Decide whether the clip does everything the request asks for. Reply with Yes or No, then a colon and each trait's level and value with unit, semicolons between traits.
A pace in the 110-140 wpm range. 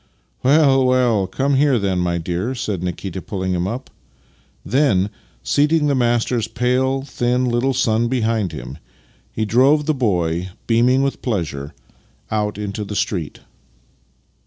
Yes: slow, 135 wpm